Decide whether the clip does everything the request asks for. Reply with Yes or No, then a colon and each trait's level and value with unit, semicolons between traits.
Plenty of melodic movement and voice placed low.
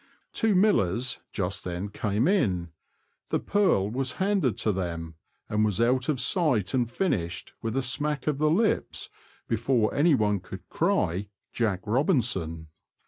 Yes: wide, 7.4 semitones; low, 115 Hz